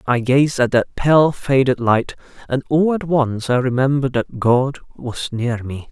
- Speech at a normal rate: Yes, average, 185 wpm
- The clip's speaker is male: Yes, male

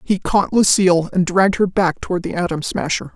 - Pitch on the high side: No, medium, 180 Hz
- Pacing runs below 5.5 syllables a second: No, 5.6 syllables/s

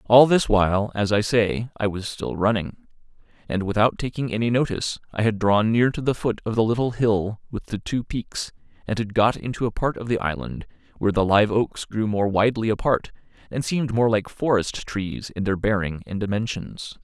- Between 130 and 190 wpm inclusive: No, fast, 205 wpm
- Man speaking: Yes, male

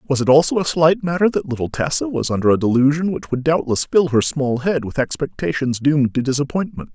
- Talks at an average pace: No, fast, 215 wpm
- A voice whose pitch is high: No, medium, 145 Hz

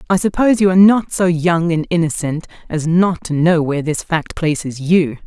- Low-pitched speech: No, medium, 170 Hz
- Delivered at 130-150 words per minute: No, fast, 205 wpm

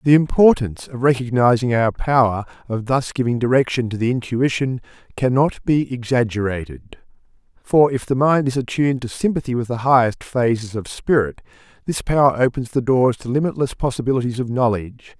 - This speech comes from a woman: No, male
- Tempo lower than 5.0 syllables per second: No, 5.5 syllables/s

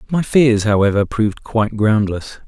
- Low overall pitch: Yes, low, 110 Hz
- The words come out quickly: No, average, 145 wpm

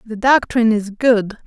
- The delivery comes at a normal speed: Yes, average, 165 wpm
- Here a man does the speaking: No, female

